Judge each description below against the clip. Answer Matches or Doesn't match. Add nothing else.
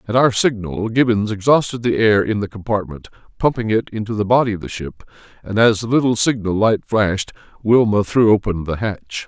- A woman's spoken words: Doesn't match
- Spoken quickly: Doesn't match